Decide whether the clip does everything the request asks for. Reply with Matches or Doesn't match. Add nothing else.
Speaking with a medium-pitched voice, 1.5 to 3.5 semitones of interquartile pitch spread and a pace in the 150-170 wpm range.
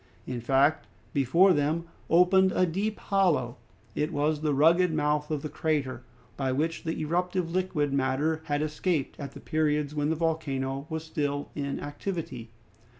Matches